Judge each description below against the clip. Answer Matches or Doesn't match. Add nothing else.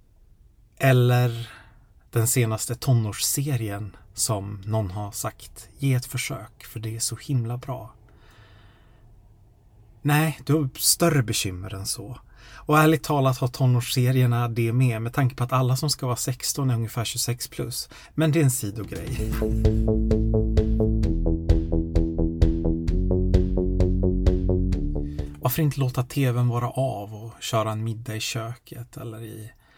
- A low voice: Matches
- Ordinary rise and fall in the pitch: Matches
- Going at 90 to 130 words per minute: Matches